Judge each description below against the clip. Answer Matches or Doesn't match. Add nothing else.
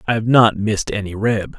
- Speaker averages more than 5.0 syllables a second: Matches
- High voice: Doesn't match